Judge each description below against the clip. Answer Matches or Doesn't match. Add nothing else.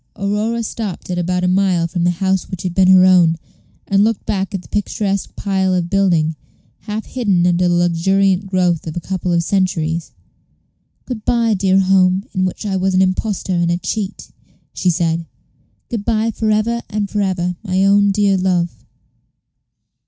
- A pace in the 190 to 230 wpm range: Doesn't match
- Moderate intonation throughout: Doesn't match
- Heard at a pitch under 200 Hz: Matches